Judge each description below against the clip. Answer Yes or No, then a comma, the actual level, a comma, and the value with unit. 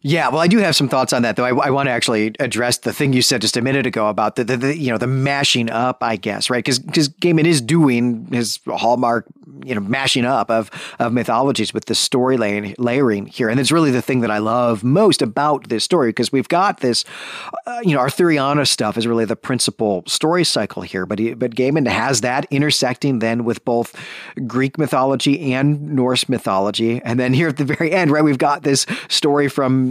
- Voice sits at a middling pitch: No, low, 130 Hz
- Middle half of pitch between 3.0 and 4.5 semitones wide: Yes, average, 3.6 semitones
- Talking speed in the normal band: No, fast, 220 wpm